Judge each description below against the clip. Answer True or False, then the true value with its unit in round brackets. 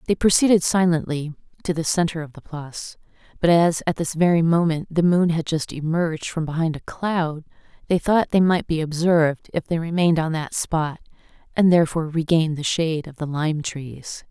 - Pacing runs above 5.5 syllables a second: False (5.4 syllables/s)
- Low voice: False (165 Hz)